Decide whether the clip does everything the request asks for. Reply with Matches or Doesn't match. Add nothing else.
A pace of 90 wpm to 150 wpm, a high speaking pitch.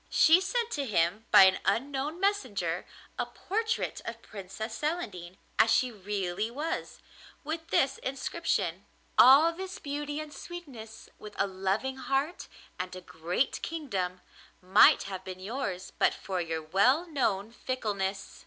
Matches